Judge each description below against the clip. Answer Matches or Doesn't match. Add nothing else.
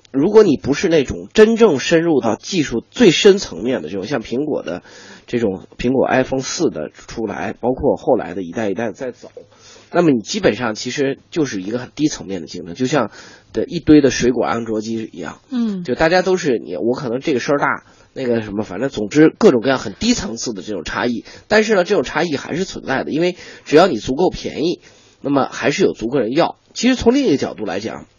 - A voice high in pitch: Doesn't match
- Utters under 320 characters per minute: Doesn't match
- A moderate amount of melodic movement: Doesn't match